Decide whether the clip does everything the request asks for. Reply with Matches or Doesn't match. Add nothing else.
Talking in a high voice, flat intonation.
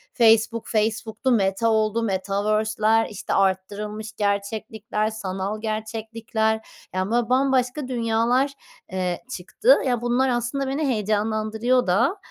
Matches